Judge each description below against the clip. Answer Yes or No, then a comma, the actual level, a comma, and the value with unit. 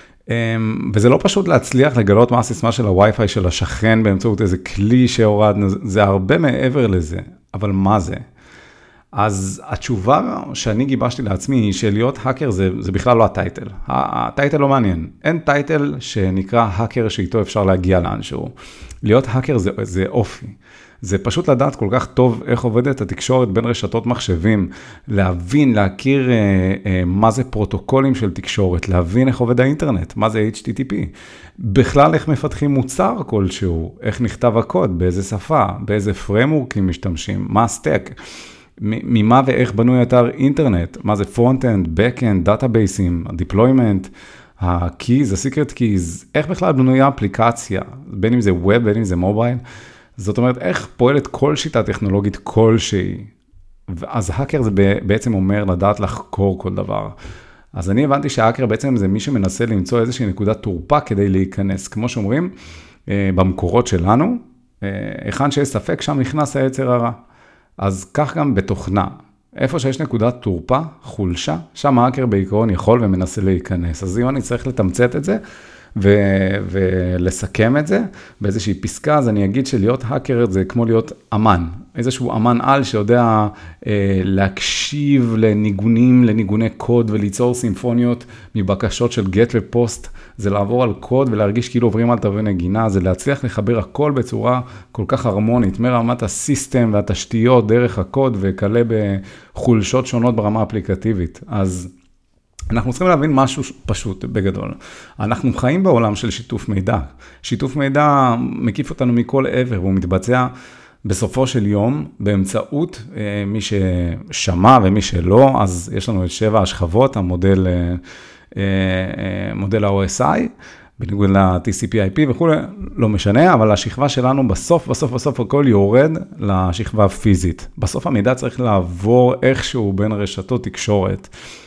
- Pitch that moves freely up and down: No, average, 4.4 semitones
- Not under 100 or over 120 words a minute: No, average, 140 wpm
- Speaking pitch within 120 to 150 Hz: No, low, 110 Hz